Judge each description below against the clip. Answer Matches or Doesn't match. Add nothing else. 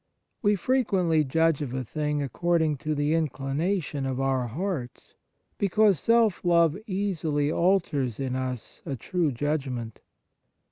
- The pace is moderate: Doesn't match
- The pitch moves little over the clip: Doesn't match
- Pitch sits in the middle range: Matches